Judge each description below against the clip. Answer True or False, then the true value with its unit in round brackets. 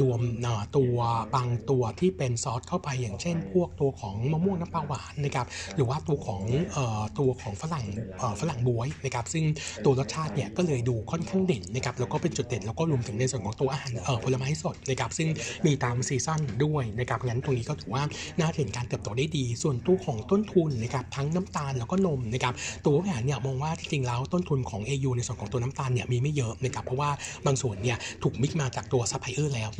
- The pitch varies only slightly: False (3.6 semitones)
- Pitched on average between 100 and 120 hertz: False (135 Hz)